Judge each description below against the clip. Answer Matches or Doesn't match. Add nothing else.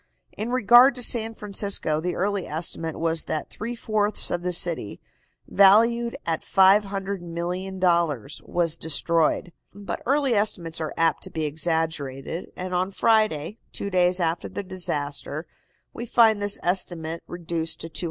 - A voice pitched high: Doesn't match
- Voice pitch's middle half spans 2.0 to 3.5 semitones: Doesn't match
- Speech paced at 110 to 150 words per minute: Matches